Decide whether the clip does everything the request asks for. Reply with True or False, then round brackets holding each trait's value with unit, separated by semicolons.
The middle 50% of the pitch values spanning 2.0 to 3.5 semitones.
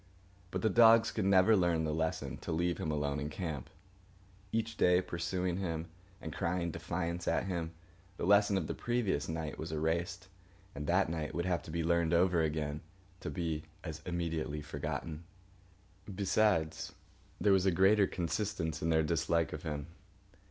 True (2.8 semitones)